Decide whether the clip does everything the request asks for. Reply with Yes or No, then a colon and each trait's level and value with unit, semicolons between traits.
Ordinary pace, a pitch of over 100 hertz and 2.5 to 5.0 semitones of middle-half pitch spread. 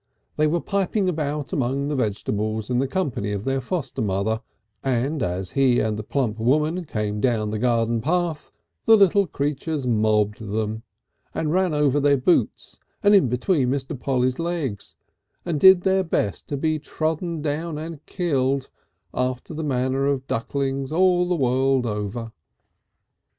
No: average, 155 wpm; low, 135 Hz; wide, 5.4 semitones